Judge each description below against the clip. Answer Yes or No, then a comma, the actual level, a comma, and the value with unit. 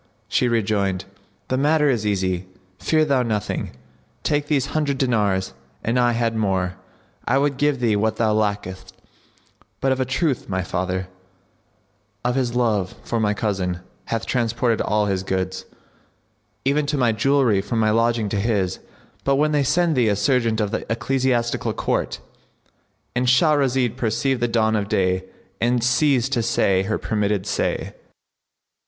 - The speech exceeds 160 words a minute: No, average, 155 wpm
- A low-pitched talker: Yes, low, 115 Hz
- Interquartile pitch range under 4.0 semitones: No, average, 4.4 semitones